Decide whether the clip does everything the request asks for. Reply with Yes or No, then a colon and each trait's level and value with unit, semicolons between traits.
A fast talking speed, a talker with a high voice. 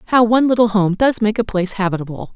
Yes: fast, 230 wpm; high, 210 Hz